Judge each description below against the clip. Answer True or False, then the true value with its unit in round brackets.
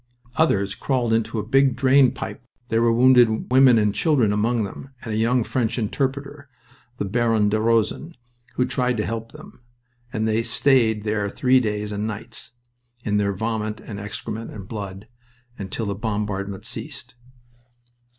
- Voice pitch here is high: False (110 Hz)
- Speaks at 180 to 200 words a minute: False (160 wpm)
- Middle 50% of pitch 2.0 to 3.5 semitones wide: True (3.0 semitones)